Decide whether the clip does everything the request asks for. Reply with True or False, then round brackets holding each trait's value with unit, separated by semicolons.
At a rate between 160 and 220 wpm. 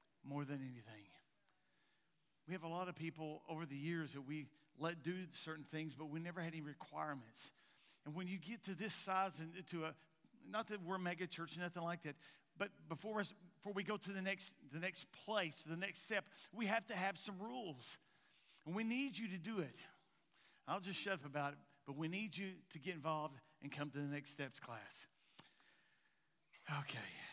True (200 wpm)